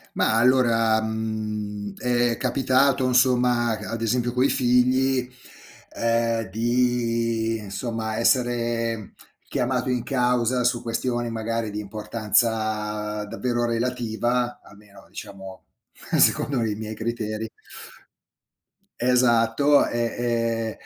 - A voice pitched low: Yes, low, 115 Hz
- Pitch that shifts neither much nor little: No, narrow, 2.0 semitones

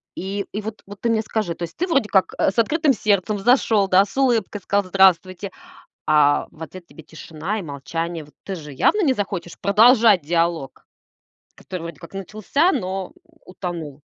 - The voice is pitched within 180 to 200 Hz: Yes, high, 190 Hz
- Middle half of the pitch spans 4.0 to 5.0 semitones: Yes, average, 4.3 semitones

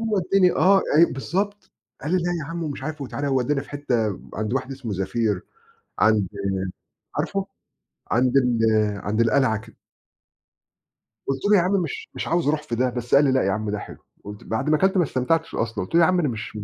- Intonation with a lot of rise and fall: Yes, wide, 6.8 semitones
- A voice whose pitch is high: No, low, 135 Hz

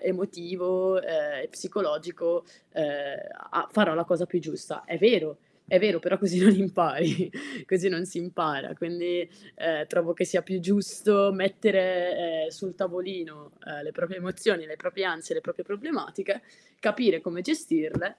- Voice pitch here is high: No, medium, 180 Hz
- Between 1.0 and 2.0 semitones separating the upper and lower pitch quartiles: No, narrow, 2.6 semitones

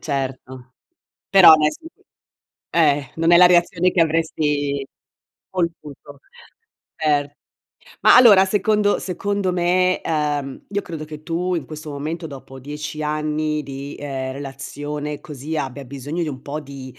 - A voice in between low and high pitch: Yes, medium, 150 Hz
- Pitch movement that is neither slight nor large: Yes, average, 3.3 semitones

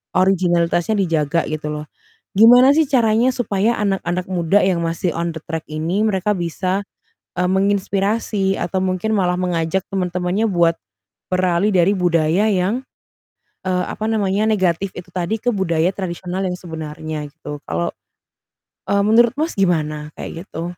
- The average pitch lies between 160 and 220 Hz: Yes, medium, 185 Hz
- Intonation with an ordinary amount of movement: Yes, average, 3.1 semitones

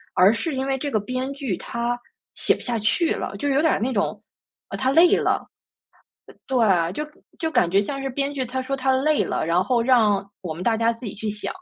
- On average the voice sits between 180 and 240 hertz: No, very high, 250 Hz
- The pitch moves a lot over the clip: No, average, 4.6 semitones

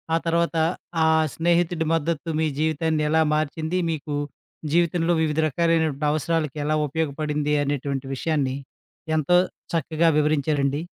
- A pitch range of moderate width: No, narrow, 2.0 semitones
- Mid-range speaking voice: Yes, medium, 155 Hz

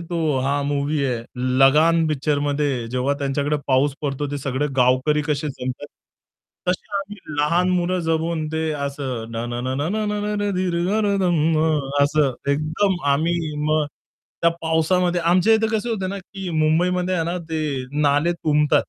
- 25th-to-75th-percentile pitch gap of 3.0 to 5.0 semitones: Yes, average, 3.7 semitones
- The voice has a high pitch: No, medium, 155 Hz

